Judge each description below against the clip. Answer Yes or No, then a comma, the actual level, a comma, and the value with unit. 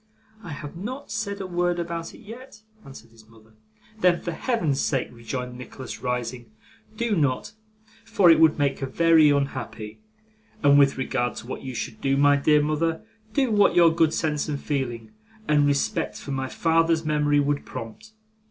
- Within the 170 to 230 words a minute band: Yes, average, 175 wpm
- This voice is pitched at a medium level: Yes, medium, 145 Hz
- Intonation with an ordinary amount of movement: Yes, average, 4.5 semitones